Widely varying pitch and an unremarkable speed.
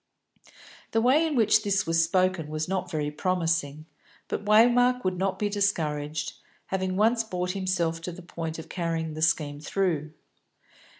No: average, 3.9 semitones; average, 160 wpm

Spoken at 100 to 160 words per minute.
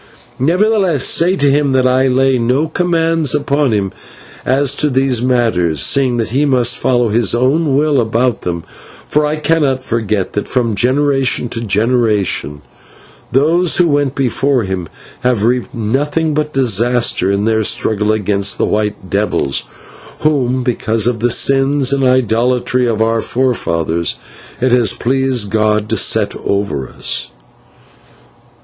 Yes: average, 145 wpm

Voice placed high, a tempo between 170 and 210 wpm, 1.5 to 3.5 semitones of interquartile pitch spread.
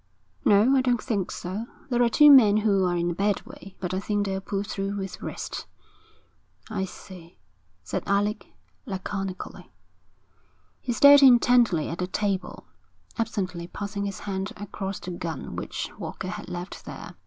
No: high, 200 Hz; average, 160 wpm; average, 2.8 semitones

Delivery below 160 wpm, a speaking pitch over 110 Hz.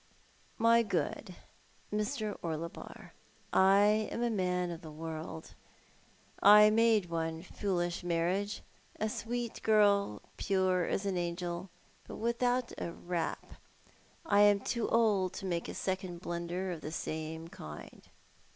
Yes: average, 140 wpm; medium, 185 Hz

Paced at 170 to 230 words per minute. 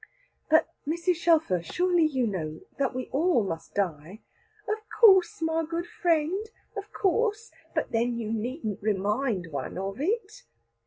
No: average, 145 wpm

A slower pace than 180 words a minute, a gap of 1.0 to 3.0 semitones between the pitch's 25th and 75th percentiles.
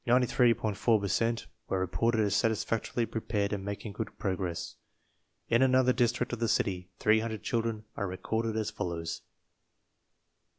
Yes: average, 155 wpm; average, 2.7 semitones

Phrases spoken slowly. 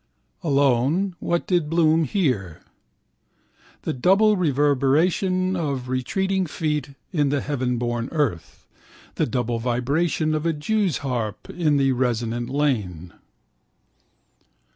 Yes: slow, 105 wpm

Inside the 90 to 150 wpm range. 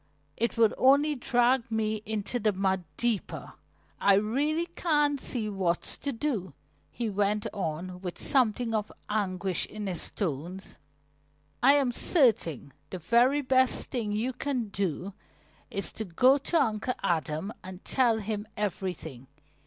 Yes: average, 140 wpm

